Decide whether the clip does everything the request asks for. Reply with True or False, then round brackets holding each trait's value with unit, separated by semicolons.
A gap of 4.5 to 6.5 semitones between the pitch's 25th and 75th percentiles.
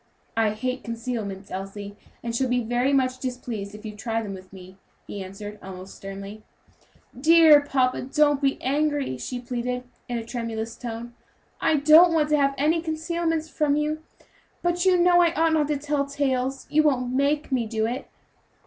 True (5.1 semitones)